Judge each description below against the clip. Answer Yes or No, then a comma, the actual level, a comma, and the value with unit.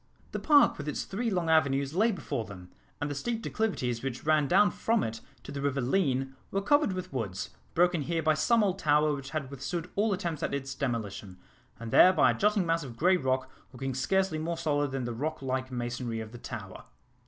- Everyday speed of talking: No, fast, 215 wpm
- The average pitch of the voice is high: No, medium, 145 Hz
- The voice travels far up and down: Yes, wide, 5.8 semitones